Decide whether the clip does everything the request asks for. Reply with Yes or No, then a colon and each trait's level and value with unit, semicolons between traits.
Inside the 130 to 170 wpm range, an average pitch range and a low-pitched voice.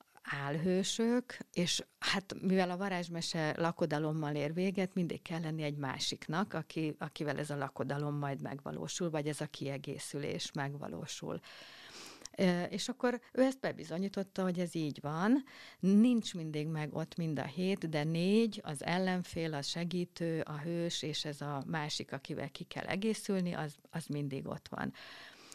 No: average, 150 wpm; average, 4.4 semitones; medium, 165 Hz